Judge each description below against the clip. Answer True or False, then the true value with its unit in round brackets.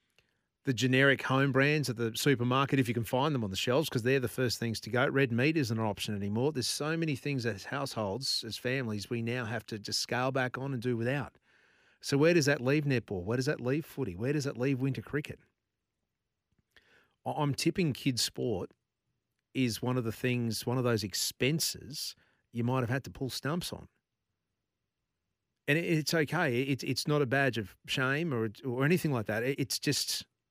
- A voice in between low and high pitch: False (130 Hz)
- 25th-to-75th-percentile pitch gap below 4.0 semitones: True (3.4 semitones)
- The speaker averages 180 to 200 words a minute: True (195 wpm)